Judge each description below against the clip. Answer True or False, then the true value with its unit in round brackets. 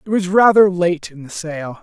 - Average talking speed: False (230 wpm)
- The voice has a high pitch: False (180 Hz)